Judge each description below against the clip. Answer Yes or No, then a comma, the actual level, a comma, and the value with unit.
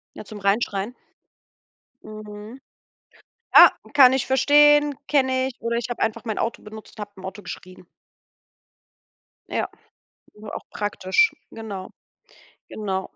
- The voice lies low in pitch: No, high, 220 Hz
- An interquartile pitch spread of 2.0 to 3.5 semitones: No, average, 4.2 semitones